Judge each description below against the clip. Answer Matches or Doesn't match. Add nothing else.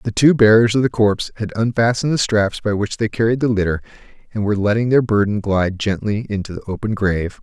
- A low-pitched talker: Matches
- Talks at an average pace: Doesn't match